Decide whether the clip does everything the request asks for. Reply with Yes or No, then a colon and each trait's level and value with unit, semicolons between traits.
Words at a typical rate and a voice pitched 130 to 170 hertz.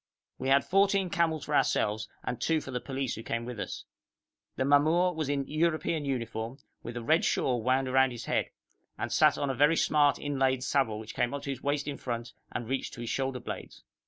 No: fast, 215 wpm; low, 135 Hz